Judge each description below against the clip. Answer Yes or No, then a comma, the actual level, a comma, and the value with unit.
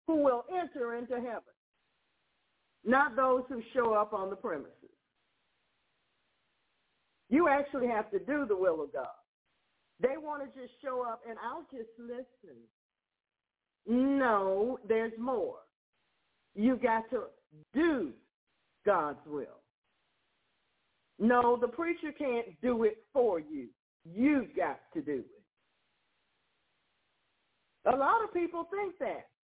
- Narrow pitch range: No, average, 4.7 semitones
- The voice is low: No, very high, 255 Hz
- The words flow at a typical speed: No, slow, 120 wpm